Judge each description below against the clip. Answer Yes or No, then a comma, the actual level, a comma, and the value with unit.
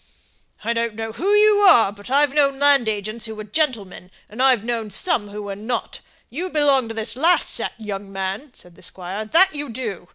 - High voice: Yes, high, 230 Hz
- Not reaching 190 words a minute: No, fast, 205 wpm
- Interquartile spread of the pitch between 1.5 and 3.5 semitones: No, wide, 5.5 semitones